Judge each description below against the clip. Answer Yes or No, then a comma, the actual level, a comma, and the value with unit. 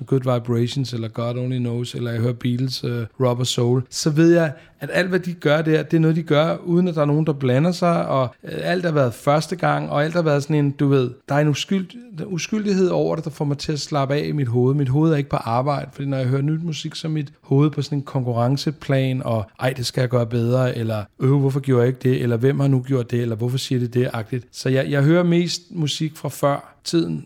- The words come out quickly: Yes, fast, 270 wpm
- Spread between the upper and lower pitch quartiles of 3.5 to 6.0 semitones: Yes, average, 3.9 semitones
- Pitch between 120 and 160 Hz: Yes, medium, 140 Hz